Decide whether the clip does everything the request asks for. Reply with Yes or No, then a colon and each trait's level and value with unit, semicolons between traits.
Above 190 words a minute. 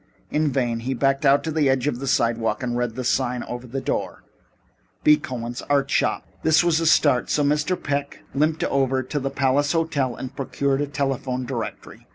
Yes: average, 200 wpm